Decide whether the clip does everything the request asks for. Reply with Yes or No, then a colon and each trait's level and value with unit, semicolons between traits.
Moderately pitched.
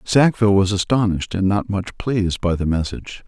No: low, 100 Hz